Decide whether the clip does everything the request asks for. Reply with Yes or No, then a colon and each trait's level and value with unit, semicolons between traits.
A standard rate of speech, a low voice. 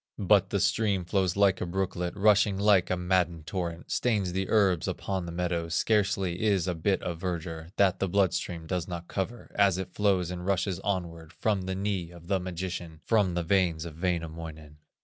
Yes: average, 190 wpm; very low, 90 Hz